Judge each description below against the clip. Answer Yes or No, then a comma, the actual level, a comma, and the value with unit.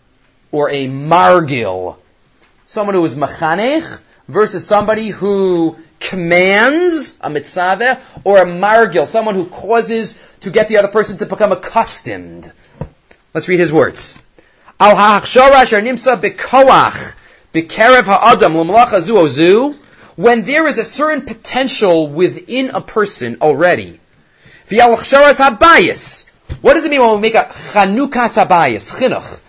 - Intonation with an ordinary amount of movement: No, wide, 6.2 semitones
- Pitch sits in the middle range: No, high, 205 Hz